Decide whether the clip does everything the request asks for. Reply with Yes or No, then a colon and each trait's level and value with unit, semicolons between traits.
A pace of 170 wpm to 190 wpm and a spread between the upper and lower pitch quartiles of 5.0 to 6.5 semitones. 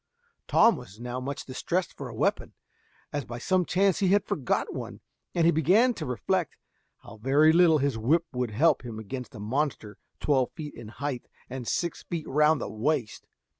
Yes: average, 185 wpm; wide, 5.4 semitones